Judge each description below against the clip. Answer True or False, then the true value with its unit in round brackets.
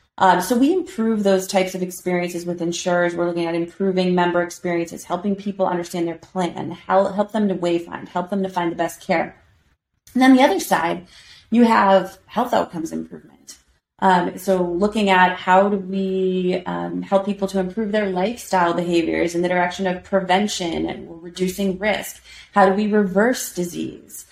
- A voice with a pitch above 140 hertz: True (185 Hz)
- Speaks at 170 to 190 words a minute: True (175 wpm)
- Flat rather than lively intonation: True (2.2 semitones)